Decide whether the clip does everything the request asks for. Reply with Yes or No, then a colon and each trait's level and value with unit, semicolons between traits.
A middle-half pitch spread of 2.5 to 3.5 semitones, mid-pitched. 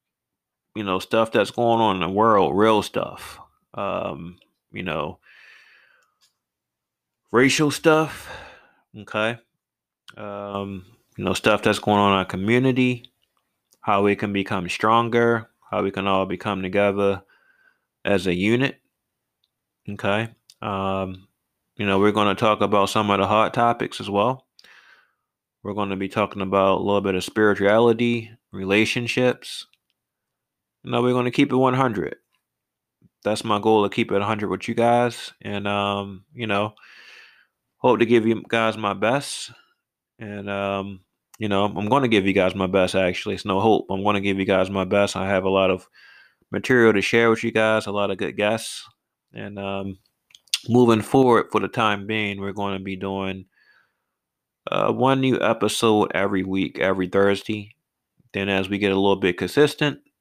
No: average, 2.8 semitones; low, 105 Hz